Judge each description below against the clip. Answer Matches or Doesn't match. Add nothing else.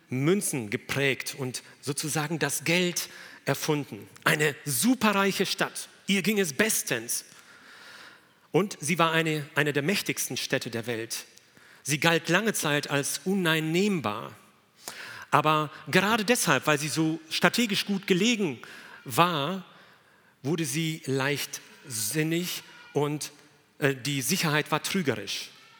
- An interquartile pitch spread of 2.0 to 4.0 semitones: Doesn't match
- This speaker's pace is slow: Matches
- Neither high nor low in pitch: Matches